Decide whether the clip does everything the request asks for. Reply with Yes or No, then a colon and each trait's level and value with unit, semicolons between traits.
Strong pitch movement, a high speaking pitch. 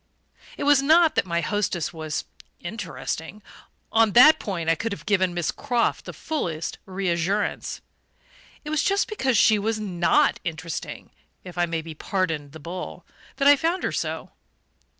Yes: wide, 6.4 semitones; high, 195 Hz